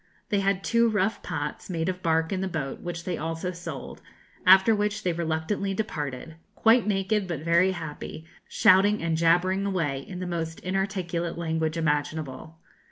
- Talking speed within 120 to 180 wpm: Yes, average, 165 wpm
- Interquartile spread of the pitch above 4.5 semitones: No, average, 3.1 semitones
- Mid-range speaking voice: Yes, medium, 175 Hz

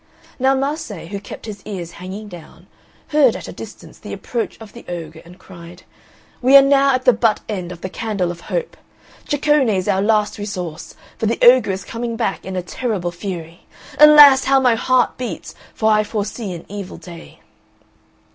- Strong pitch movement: Yes, wide, 5.8 semitones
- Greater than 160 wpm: Yes, average, 185 wpm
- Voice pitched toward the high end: Yes, high, 210 Hz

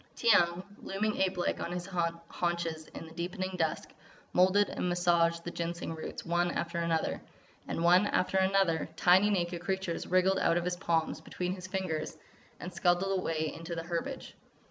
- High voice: No, medium, 175 Hz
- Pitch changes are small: Yes, narrow, 1.9 semitones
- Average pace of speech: Yes, average, 165 wpm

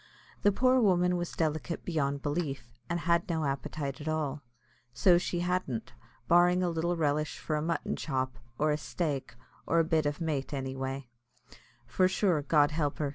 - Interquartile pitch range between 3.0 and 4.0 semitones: Yes, average, 3.6 semitones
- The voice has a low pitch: No, medium, 155 Hz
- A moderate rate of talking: Yes, average, 175 wpm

